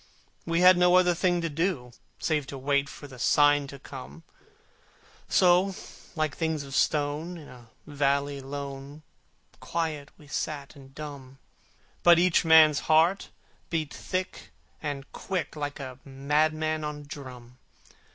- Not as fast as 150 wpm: Yes, average, 140 wpm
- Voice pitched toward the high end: No, medium, 150 Hz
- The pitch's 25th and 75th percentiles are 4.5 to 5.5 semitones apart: No, average, 2.8 semitones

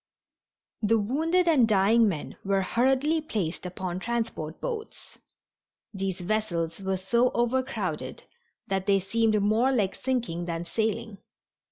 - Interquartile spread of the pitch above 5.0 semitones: No, average, 4.3 semitones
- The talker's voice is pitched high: Yes, high, 215 Hz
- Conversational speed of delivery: No, slow, 125 wpm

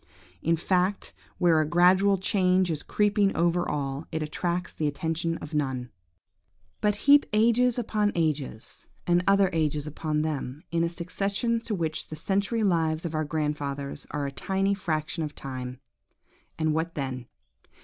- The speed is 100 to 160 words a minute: Yes, average, 155 wpm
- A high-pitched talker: No, medium, 165 Hz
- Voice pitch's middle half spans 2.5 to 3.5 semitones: No, average, 4.3 semitones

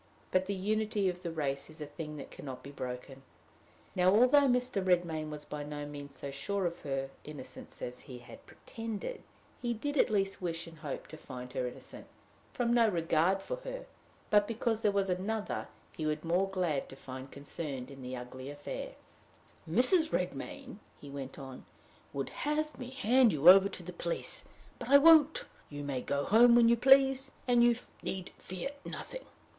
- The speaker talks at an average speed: Yes, average, 190 wpm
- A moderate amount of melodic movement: No, wide, 8.4 semitones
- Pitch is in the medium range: Yes, medium, 180 Hz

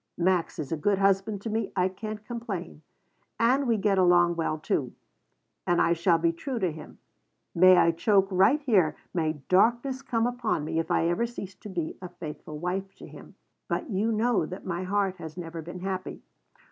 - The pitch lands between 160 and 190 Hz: Yes, medium, 185 Hz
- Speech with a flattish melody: No, average, 4.1 semitones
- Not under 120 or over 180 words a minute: No, average, 195 wpm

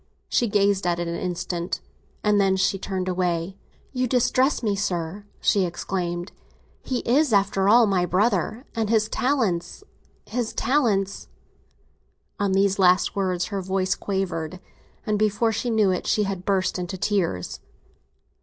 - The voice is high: Yes, high, 195 Hz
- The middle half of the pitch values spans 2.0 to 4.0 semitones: Yes, average, 2.9 semitones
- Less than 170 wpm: Yes, average, 145 wpm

